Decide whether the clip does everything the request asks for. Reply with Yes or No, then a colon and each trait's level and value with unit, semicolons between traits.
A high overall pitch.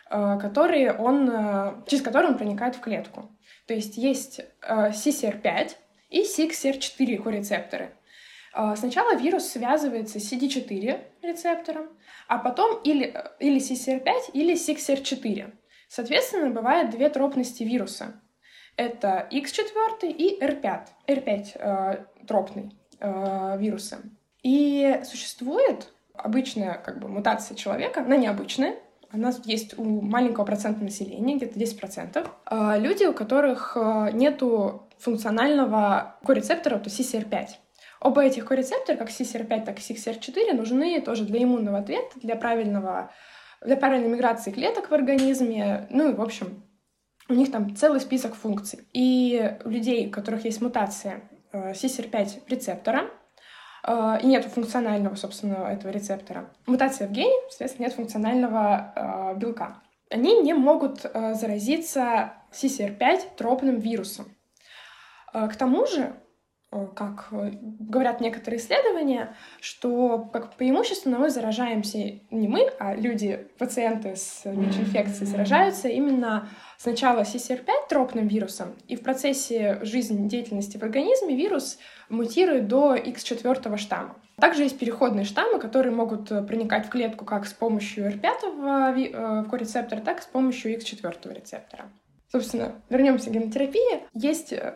Yes: high, 235 Hz